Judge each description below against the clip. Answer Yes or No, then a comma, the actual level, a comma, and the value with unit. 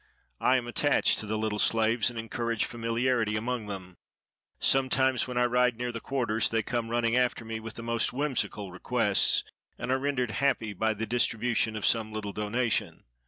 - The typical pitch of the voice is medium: No, low, 115 Hz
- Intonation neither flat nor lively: No, narrow, 2.2 semitones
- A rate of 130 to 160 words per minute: No, average, 180 wpm